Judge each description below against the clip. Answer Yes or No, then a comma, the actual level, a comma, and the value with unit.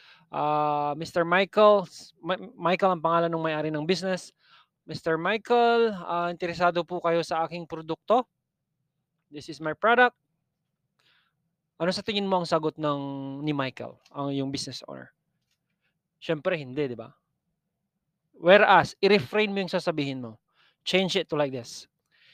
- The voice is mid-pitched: Yes, medium, 165 Hz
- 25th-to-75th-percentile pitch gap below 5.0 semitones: Yes, average, 3.6 semitones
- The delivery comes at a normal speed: Yes, average, 135 wpm